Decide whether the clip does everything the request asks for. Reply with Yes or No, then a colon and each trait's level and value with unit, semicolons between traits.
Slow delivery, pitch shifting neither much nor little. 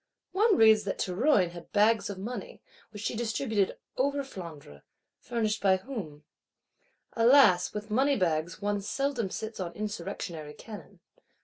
Yes: slow, 130 wpm; average, 4.5 semitones